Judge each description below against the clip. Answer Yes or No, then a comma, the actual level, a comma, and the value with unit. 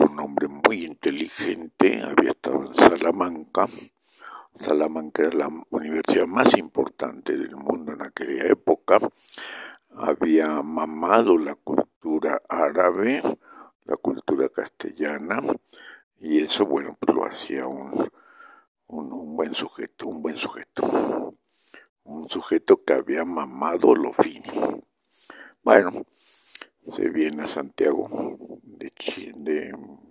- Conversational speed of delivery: No, slow, 100 wpm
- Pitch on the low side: No, very high, 345 Hz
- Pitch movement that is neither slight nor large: No, wide, 7.2 semitones